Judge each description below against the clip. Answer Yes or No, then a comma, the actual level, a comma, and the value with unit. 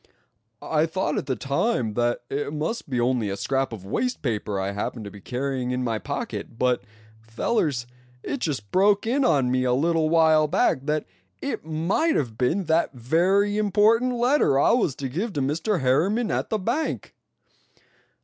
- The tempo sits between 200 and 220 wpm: No, average, 180 wpm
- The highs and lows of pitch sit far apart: Yes, wide, 8.1 semitones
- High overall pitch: No, medium, 150 Hz